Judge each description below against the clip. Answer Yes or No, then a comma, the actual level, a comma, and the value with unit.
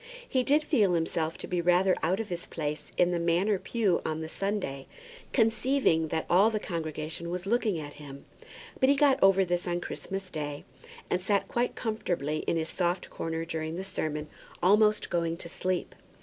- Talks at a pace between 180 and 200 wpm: Yes, average, 185 wpm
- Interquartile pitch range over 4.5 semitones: No, average, 4.0 semitones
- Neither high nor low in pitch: Yes, medium, 175 Hz